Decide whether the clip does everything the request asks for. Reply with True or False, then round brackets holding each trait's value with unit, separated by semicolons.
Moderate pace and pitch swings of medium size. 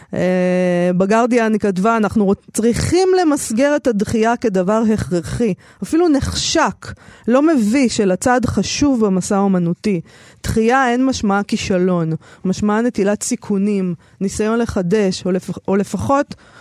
True (115 wpm; 4.1 semitones)